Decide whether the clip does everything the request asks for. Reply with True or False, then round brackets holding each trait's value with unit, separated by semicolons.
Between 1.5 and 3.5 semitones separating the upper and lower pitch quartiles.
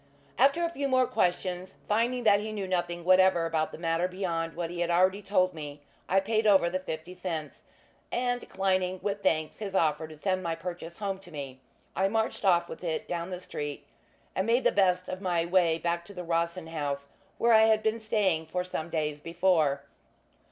True (3.2 semitones)